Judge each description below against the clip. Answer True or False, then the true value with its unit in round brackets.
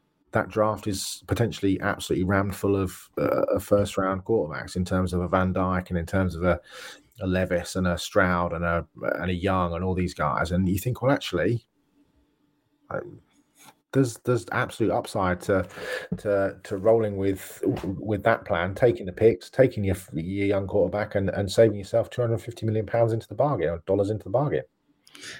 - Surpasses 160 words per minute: True (190 wpm)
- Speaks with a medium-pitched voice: False (95 Hz)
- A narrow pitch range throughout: False (3.1 semitones)